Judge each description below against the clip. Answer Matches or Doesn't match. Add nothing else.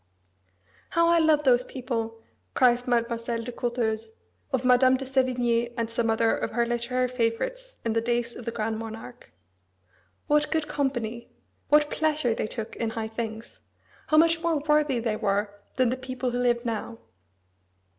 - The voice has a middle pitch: Doesn't match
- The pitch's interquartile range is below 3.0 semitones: Matches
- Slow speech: Doesn't match